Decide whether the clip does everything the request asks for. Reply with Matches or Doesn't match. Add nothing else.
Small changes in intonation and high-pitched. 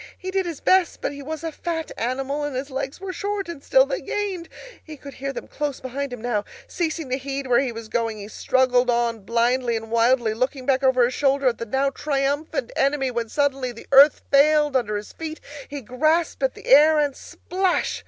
Doesn't match